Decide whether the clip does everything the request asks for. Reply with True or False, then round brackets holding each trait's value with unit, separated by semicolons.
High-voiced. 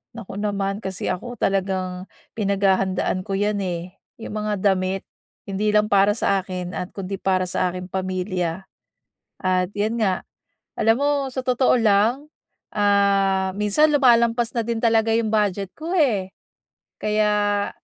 True (200 Hz)